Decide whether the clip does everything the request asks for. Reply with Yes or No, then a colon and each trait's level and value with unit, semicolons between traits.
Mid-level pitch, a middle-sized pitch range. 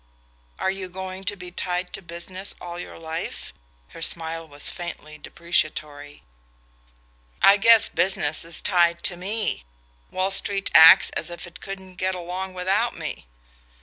No: medium, 180 Hz; narrow, 2.3 semitones